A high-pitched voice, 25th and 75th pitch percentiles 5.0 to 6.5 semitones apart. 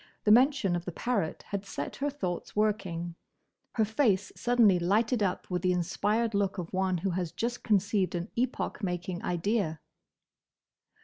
No: high, 195 Hz; average, 3.8 semitones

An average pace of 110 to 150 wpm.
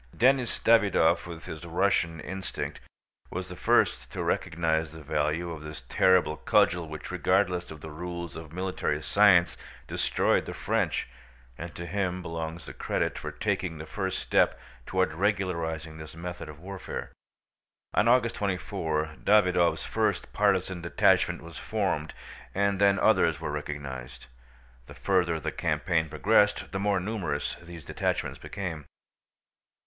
Yes: average, 140 wpm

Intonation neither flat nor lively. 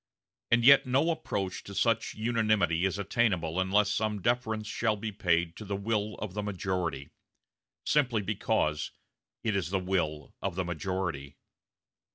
Yes: average, 3.5 semitones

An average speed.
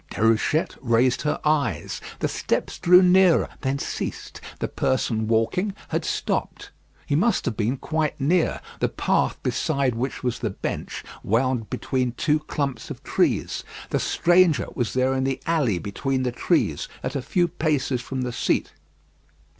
Yes: average, 155 wpm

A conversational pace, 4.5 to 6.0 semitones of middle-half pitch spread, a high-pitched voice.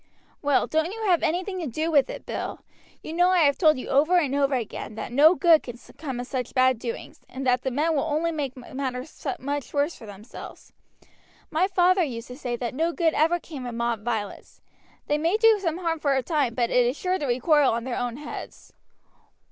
No: fast, 220 wpm; average, 4.8 semitones; very high, 285 Hz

